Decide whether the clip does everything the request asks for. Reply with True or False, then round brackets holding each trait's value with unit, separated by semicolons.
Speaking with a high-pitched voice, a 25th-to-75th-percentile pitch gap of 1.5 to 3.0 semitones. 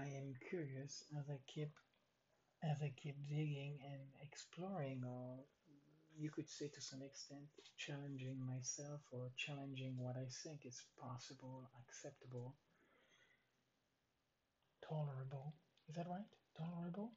False (140 Hz; 2.4 semitones)